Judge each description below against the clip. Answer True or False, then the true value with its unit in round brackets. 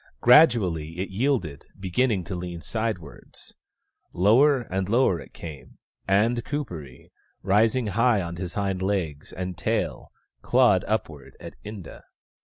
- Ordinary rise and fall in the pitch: True (4.9 semitones)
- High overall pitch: False (95 Hz)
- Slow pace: True (125 wpm)